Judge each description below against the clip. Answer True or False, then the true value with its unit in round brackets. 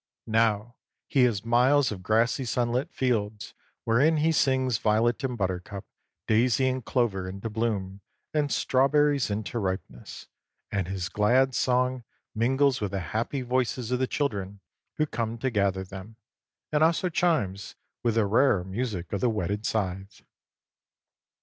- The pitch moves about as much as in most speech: True (4.4 semitones)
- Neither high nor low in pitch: False (115 Hz)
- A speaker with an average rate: True (145 wpm)